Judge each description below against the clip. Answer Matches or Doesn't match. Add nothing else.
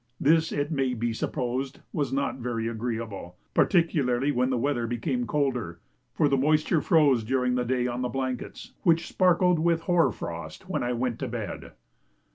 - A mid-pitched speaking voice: Doesn't match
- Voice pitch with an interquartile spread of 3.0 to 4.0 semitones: Matches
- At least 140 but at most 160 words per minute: Doesn't match